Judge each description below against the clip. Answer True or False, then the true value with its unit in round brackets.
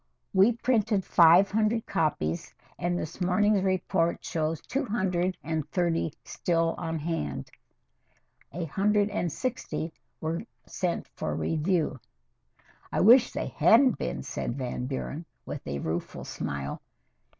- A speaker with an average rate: False (130 wpm)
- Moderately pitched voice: True (175 Hz)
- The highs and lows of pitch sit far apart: False (4.4 semitones)